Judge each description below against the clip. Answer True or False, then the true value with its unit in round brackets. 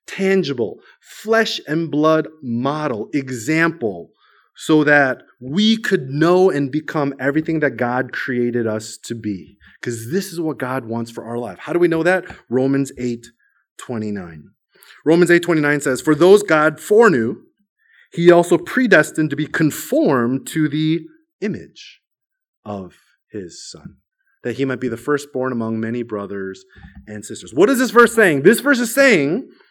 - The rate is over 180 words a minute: False (150 wpm)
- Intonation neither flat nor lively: False (6.2 semitones)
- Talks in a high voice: False (150 Hz)